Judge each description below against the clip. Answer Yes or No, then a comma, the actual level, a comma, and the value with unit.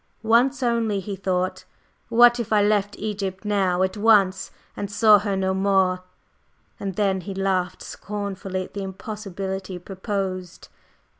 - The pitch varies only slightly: Yes, narrow, 1.8 semitones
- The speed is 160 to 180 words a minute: No, average, 140 wpm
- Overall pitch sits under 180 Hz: No, high, 195 Hz